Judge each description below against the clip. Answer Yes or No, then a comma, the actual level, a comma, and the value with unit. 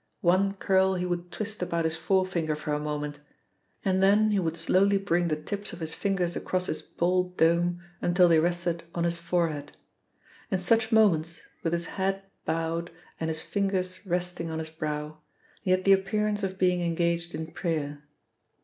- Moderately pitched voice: Yes, medium, 175 Hz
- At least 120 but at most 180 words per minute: Yes, average, 175 wpm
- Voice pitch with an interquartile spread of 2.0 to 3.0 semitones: Yes, average, 2.7 semitones